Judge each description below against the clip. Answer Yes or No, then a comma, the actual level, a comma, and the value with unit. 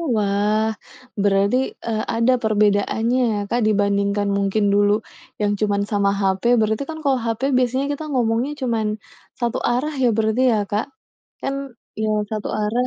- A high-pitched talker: Yes, high, 215 Hz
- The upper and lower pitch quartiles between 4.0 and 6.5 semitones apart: No, average, 2.8 semitones